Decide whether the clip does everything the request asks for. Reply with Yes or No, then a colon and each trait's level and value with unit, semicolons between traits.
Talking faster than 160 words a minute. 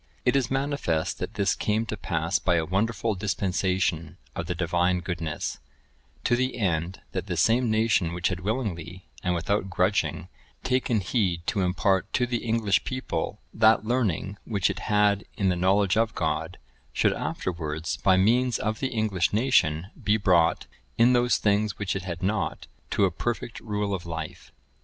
Yes: average, 170 wpm